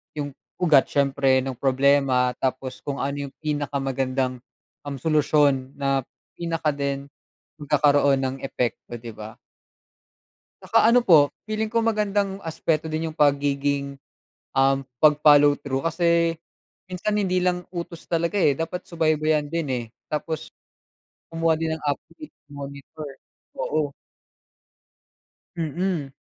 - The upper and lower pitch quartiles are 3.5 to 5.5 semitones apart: No, average, 3.1 semitones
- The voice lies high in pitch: No, medium, 145 Hz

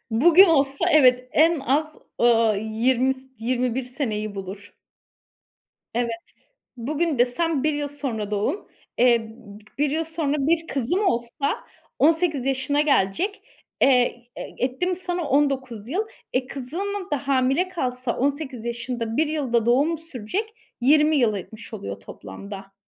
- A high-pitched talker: Yes, very high, 265 Hz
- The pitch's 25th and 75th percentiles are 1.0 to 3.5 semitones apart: No, average, 4.7 semitones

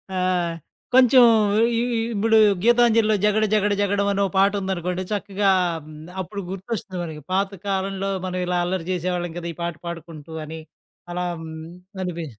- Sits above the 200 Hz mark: No, high, 190 Hz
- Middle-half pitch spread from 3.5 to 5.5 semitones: No, narrow, 2.6 semitones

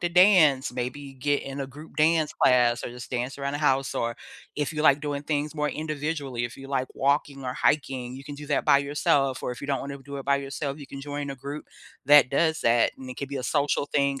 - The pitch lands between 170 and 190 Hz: No, medium, 140 Hz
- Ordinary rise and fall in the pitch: No, narrow, 1.7 semitones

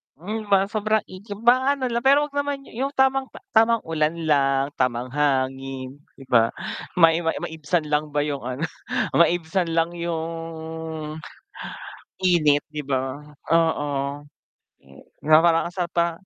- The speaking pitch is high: No, medium, 165 Hz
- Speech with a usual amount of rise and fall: No, wide, 6.3 semitones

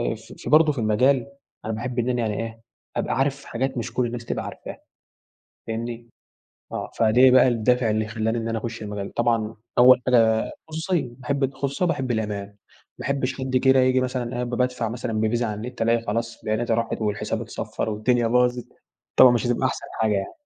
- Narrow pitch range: Yes, narrow, 2.3 semitones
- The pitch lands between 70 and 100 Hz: No, low, 120 Hz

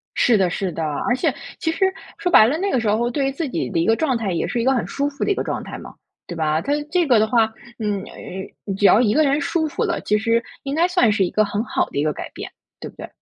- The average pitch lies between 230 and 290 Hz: Yes, high, 235 Hz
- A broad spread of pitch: Yes, wide, 6.0 semitones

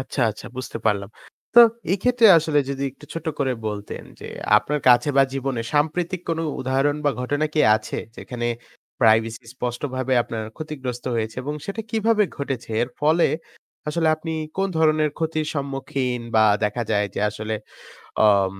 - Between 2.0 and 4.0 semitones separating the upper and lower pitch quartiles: No, average, 4.7 semitones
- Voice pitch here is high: No, low, 135 Hz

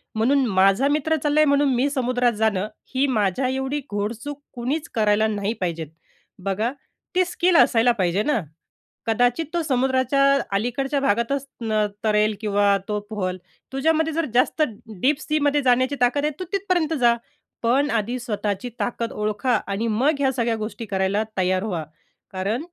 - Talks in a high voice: Yes, high, 245 Hz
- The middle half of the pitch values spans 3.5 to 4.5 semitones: No, average, 5.0 semitones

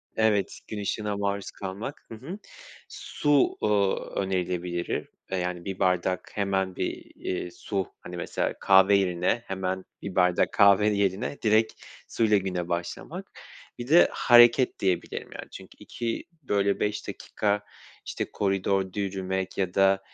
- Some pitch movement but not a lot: No, narrow, 2.2 semitones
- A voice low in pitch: Yes, very low, 95 Hz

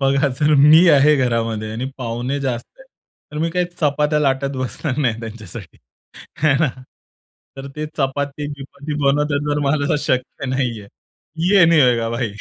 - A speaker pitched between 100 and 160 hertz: Yes, medium, 140 Hz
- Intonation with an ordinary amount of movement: Yes, average, 3.2 semitones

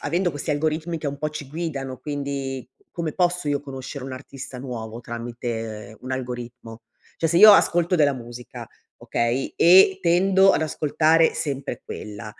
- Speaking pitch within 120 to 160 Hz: Yes, medium, 140 Hz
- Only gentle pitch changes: No, average, 4.9 semitones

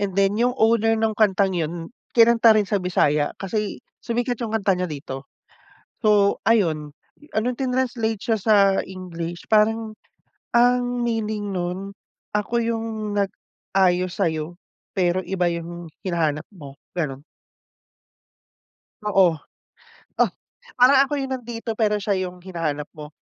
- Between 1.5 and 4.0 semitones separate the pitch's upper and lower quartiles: No, average, 4.4 semitones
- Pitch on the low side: No, high, 200 Hz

